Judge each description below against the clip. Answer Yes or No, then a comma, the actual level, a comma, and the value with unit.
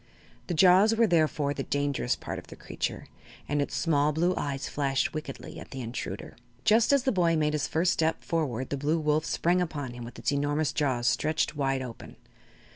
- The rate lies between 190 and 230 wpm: Yes, average, 200 wpm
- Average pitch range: Yes, average, 3.3 semitones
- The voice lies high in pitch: No, medium, 150 Hz